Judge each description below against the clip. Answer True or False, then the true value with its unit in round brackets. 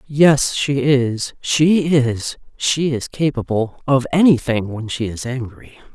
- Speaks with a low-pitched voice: True (130 Hz)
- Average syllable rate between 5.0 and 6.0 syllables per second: False (3.5 syllables/s)